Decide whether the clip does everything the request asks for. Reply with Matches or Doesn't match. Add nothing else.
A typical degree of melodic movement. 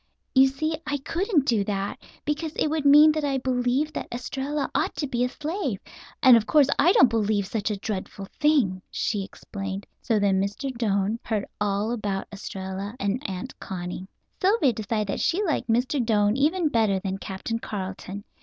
Doesn't match